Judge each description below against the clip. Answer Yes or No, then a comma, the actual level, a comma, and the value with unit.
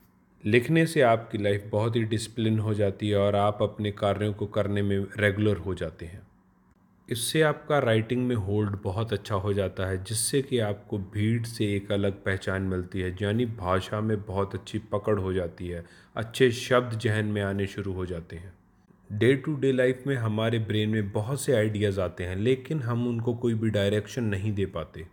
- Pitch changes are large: No, average, 2.8 semitones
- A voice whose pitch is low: Yes, low, 105 Hz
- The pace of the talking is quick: Yes, fast, 195 wpm